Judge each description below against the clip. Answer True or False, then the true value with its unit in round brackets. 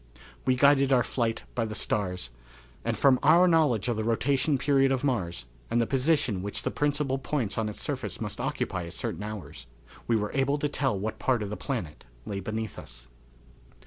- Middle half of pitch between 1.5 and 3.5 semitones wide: False (4.8 semitones)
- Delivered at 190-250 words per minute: True (195 wpm)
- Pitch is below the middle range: True (115 Hz)